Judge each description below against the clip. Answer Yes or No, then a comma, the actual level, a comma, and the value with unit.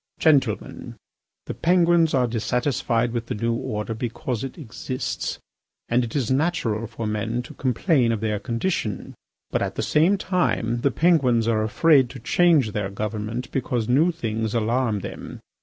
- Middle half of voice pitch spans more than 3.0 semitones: Yes, average, 3.9 semitones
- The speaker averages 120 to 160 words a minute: Yes, average, 155 wpm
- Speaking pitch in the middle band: No, low, 120 Hz